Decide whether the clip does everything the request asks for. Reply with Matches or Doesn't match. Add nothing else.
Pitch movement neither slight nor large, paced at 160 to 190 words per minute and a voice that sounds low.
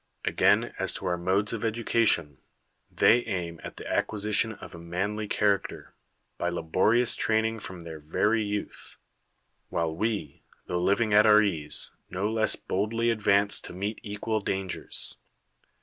Doesn't match